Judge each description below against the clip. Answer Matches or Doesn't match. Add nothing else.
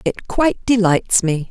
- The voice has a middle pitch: Doesn't match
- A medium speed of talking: Matches